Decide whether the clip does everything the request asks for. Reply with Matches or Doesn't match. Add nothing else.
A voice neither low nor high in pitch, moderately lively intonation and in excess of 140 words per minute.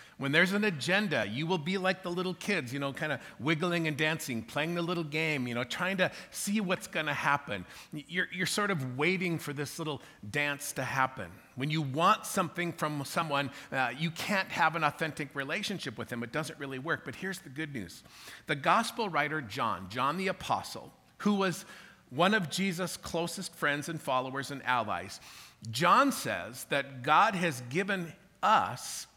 Matches